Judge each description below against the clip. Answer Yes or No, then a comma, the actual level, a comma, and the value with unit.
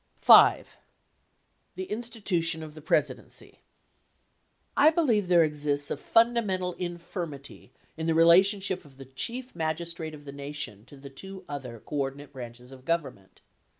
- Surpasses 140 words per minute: No, slow, 135 wpm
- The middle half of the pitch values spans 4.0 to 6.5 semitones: Yes, average, 5.1 semitones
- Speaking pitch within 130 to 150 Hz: No, medium, 160 Hz